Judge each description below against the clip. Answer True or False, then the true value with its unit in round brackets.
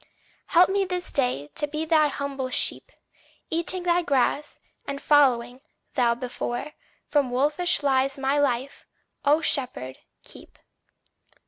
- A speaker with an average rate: False (125 wpm)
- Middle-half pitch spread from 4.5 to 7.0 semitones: False (3.4 semitones)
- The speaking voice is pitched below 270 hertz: False (280 Hz)